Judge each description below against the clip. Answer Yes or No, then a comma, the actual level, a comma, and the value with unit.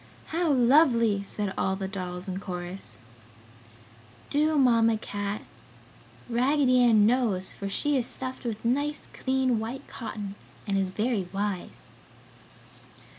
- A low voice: No, high, 225 Hz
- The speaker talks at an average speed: No, slow, 125 wpm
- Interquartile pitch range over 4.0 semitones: Yes, average, 4.7 semitones